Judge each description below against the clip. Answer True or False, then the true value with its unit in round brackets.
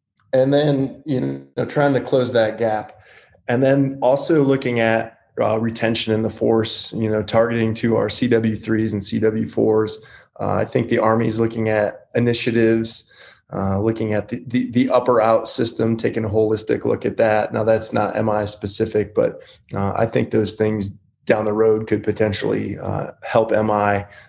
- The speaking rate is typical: True (175 wpm)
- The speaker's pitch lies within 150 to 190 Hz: False (110 Hz)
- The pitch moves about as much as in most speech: False (1.3 semitones)